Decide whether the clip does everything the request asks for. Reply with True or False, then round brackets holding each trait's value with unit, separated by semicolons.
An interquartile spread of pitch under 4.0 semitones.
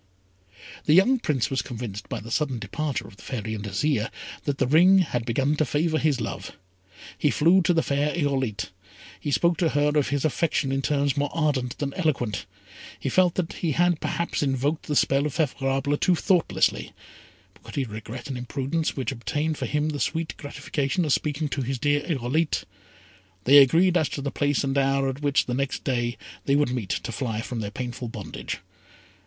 True (3.6 semitones)